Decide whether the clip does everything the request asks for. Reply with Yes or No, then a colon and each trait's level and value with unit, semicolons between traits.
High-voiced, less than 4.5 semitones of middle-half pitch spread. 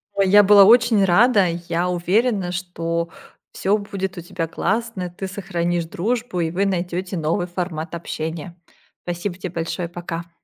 No: medium, 180 Hz; narrow, 2.6 semitones